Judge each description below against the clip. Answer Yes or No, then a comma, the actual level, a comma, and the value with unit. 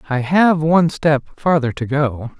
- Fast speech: No, average, 175 wpm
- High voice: No, medium, 150 Hz